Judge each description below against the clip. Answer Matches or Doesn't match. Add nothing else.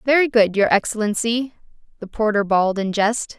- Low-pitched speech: Doesn't match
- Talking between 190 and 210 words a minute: Doesn't match